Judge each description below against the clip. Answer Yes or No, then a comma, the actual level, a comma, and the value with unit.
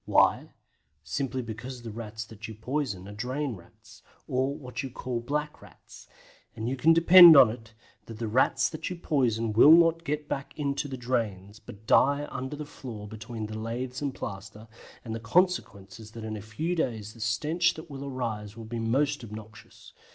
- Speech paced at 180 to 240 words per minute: Yes, average, 190 wpm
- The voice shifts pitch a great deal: No, average, 4.5 semitones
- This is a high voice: No, low, 120 Hz